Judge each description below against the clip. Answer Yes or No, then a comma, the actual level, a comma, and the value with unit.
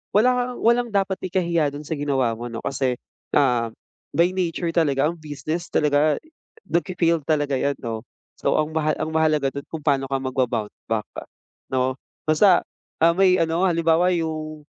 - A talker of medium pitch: Yes, medium, 155 Hz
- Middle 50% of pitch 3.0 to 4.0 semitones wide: Yes, average, 3.7 semitones